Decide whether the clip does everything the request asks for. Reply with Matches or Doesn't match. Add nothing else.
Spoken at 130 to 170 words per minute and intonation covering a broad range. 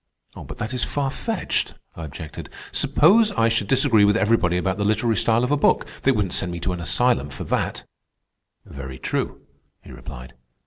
Doesn't match